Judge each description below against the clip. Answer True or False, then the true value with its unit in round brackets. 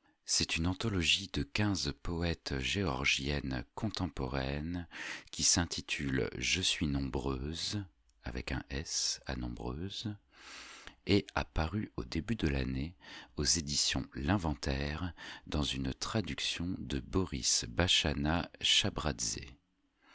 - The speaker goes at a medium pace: False (100 wpm)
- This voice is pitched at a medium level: False (75 Hz)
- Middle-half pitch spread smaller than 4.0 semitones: False (4.8 semitones)